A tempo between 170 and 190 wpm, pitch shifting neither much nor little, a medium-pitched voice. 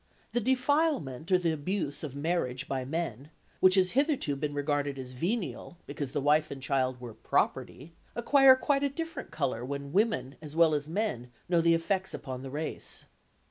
No: average, 180 wpm; wide, 6.5 semitones; medium, 155 Hz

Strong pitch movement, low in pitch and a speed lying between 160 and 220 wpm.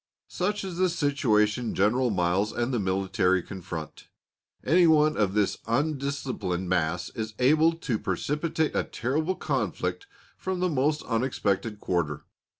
No: wide, 8.0 semitones; low, 120 Hz; slow, 135 wpm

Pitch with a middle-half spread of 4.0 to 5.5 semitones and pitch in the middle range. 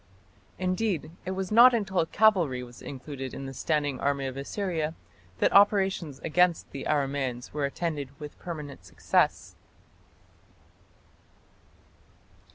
Yes: average, 5.2 semitones; medium, 150 Hz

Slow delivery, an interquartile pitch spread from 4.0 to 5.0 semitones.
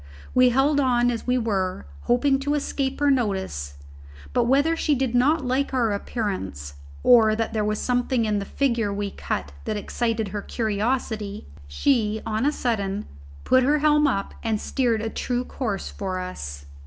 No: average, 170 wpm; average, 4.3 semitones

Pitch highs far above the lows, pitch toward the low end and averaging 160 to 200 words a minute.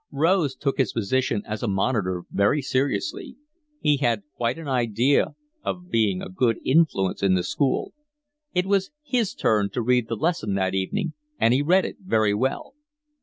Yes: wide, 6.5 semitones; low, 125 Hz; average, 170 wpm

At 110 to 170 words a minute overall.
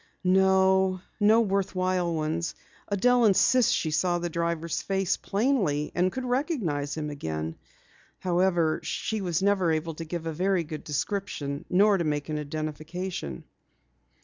Yes: average, 140 wpm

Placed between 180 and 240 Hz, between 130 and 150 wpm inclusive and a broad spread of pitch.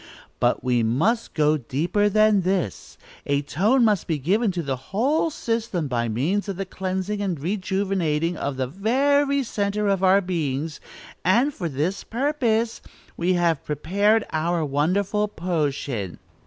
Yes: medium, 185 Hz; average, 145 wpm; wide, 5.8 semitones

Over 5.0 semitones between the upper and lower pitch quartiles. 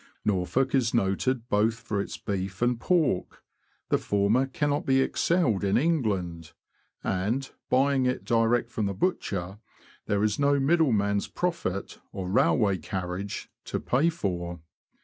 Yes: wide, 5.5 semitones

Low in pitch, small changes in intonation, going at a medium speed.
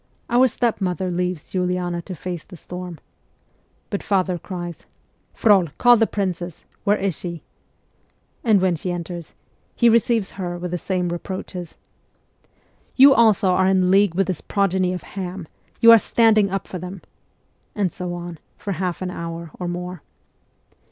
No: medium, 185 Hz; narrow, 2.1 semitones; average, 165 wpm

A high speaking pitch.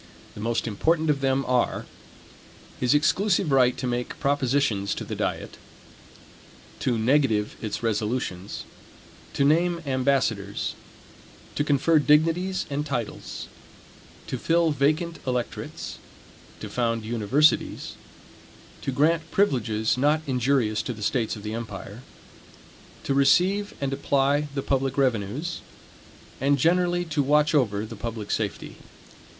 No: low, 135 Hz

